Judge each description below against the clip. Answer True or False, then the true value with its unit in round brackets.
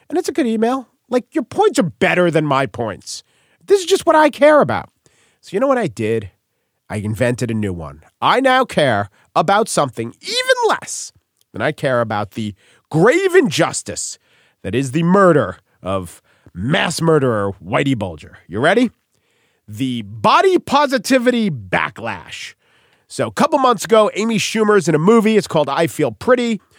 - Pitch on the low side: False (180 Hz)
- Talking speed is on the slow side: False (170 wpm)